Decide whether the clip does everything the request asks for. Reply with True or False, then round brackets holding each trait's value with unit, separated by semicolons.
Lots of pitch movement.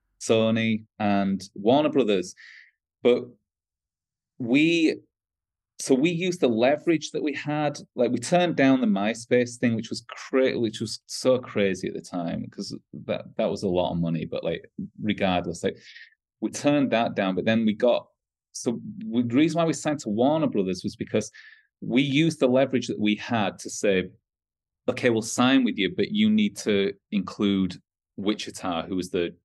True (6.6 semitones)